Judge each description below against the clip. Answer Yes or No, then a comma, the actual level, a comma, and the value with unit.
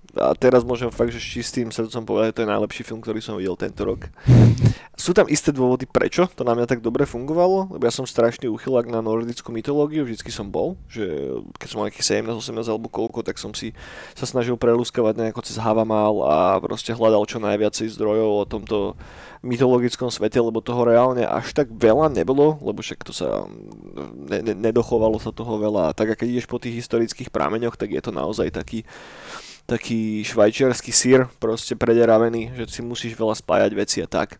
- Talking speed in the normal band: No, fast, 195 wpm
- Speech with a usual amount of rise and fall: No, narrow, 2.0 semitones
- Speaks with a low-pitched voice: Yes, low, 115 Hz